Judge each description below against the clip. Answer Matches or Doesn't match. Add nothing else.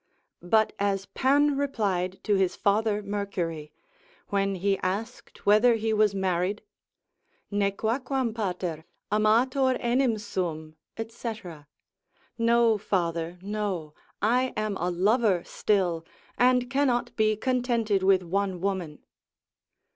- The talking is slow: Matches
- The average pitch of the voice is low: Doesn't match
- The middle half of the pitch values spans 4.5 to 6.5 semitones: Doesn't match